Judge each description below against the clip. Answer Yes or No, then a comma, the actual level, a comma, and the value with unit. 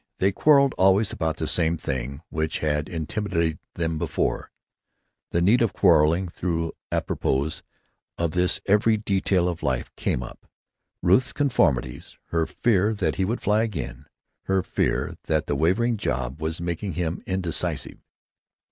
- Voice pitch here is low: Yes, very low, 85 Hz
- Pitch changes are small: No, average, 4.0 semitones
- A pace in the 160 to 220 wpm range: No, average, 145 wpm